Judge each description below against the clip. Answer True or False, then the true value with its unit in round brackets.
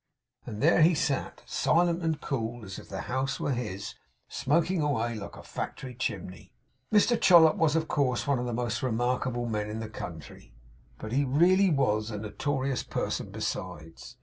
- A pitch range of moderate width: False (5.7 semitones)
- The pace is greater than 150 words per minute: True (175 wpm)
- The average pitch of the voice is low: True (125 Hz)